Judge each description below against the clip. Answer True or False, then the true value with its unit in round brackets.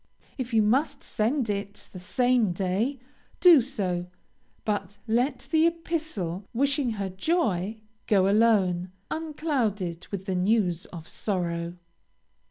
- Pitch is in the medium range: False (210 Hz)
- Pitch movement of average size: False (6.3 semitones)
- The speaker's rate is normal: False (120 wpm)